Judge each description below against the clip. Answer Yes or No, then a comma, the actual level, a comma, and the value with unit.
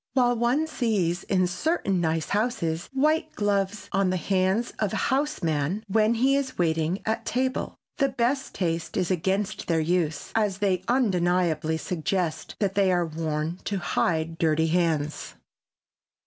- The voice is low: No, medium, 185 Hz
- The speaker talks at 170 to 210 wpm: No, average, 150 wpm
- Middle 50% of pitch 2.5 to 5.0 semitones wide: No, wide, 5.4 semitones